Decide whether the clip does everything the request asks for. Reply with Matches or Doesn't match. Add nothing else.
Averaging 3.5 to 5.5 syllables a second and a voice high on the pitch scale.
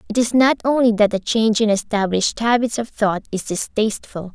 Doesn't match